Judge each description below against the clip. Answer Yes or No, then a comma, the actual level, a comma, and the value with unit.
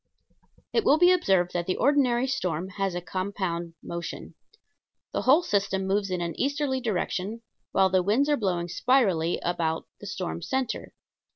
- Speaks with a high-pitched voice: Yes, high, 195 Hz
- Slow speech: No, average, 160 wpm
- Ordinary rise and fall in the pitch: No, wide, 6.7 semitones